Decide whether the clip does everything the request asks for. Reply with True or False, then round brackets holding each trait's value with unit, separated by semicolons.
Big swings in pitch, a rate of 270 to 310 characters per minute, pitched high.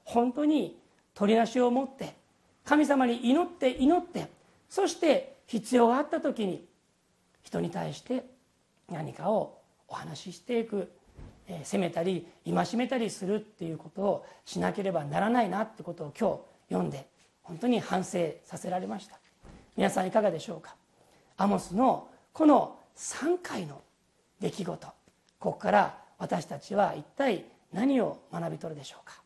True (6.4 semitones; 280 characters per minute; 235 Hz)